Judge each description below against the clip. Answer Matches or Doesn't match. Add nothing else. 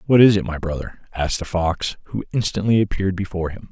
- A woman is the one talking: Doesn't match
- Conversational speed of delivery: Doesn't match